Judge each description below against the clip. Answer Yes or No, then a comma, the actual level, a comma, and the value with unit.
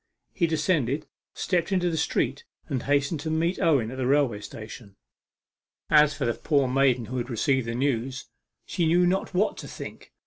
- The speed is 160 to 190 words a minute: Yes, average, 180 wpm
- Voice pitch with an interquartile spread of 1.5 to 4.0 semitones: No, average, 4.6 semitones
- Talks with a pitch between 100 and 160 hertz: Yes, medium, 140 Hz